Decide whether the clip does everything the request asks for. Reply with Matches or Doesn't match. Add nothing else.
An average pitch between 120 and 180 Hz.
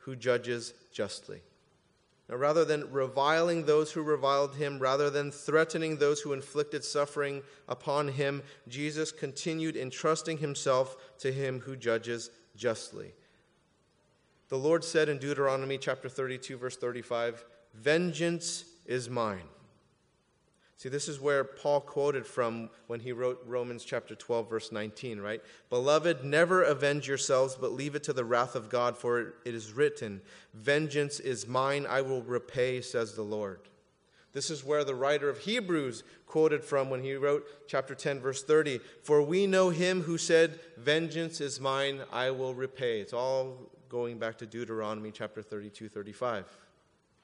Matches